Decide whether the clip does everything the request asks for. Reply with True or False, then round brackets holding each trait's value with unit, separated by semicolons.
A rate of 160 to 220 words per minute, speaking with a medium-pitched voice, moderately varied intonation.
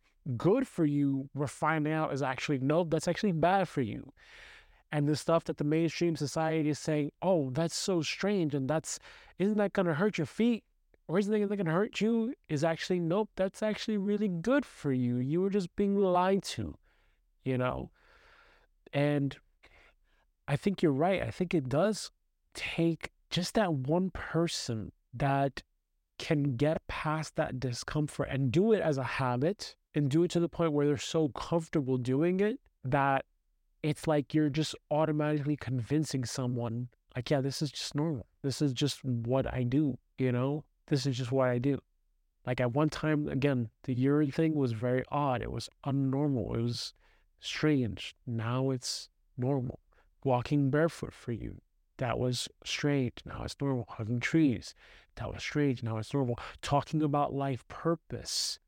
True (170 wpm; 145 Hz; 4.2 semitones)